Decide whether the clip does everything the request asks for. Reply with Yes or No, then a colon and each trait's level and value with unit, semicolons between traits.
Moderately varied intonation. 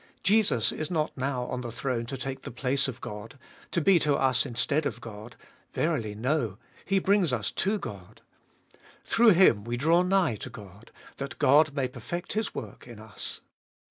No: wide, 5.9 semitones